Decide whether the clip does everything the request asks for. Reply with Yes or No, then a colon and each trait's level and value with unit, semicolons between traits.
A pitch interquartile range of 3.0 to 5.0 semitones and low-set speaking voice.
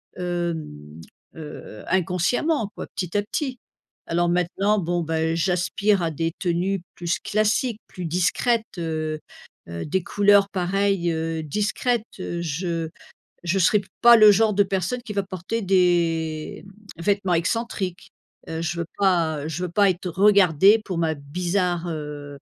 No: average, 3.6 semitones; medium, 180 Hz